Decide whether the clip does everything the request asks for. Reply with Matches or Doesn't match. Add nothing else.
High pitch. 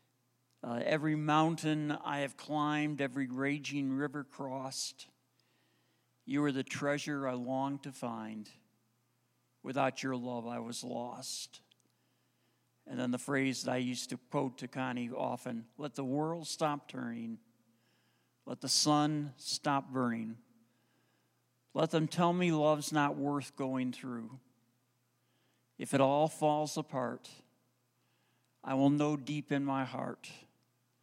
Doesn't match